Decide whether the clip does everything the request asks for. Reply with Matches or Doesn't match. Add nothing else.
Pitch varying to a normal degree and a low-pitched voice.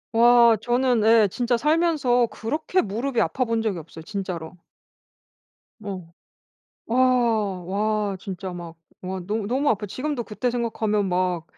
Doesn't match